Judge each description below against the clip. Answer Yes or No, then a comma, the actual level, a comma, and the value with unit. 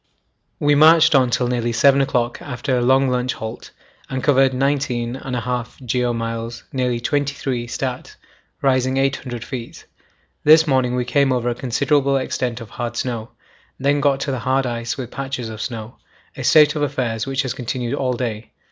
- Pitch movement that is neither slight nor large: No, narrow, 2.2 semitones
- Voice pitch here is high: No, low, 125 Hz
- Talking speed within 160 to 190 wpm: Yes, average, 170 wpm